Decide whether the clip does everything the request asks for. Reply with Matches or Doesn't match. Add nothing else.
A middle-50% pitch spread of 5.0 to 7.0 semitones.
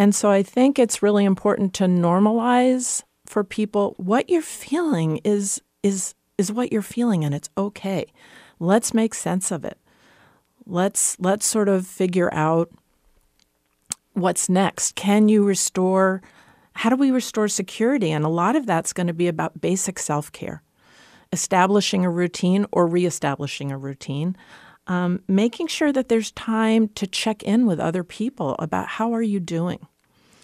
Doesn't match